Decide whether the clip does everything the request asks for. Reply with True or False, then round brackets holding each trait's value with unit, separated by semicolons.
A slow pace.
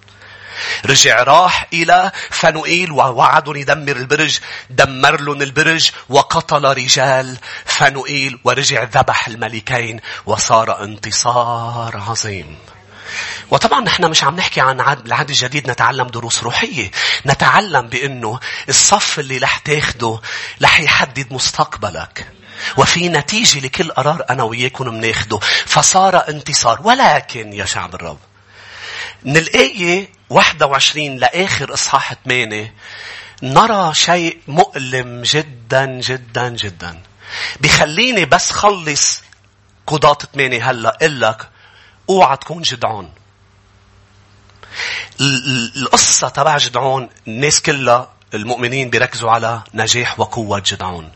True (100 wpm)